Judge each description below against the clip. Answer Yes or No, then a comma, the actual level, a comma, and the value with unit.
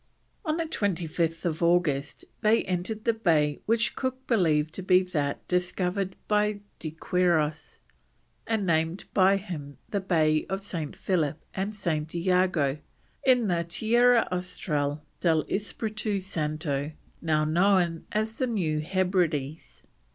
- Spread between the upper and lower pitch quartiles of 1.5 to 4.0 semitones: No, average, 4.5 semitones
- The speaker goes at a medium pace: No, slow, 125 wpm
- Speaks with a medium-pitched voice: Yes, medium, 180 Hz